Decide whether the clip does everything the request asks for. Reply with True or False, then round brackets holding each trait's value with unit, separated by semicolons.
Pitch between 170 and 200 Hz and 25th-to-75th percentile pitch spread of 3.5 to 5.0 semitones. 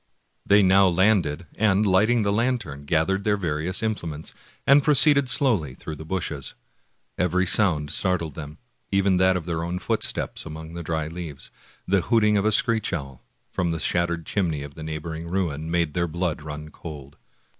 False (85 Hz; 4.1 semitones)